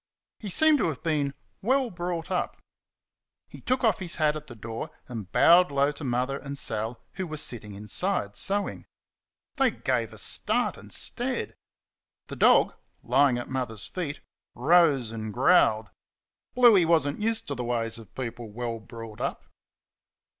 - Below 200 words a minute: Yes, average, 160 wpm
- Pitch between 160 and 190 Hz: No, medium, 140 Hz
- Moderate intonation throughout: No, wide, 7.4 semitones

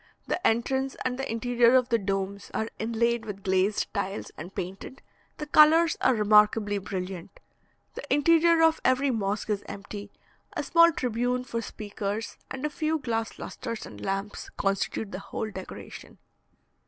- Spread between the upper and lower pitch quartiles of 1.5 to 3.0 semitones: No, average, 4.6 semitones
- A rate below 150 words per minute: No, average, 155 wpm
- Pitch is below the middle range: No, high, 225 Hz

